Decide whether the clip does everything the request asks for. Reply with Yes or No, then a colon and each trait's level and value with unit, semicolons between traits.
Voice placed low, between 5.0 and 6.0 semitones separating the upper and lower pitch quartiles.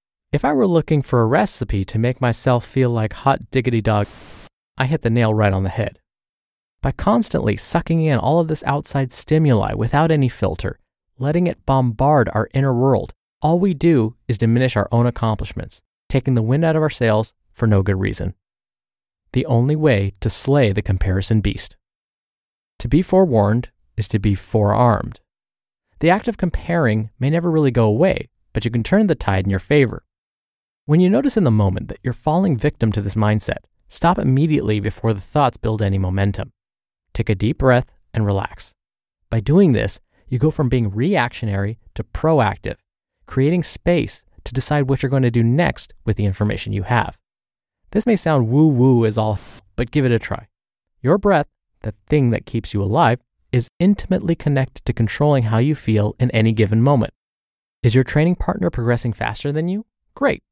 Yes: low, 120 Hz; wide, 5.4 semitones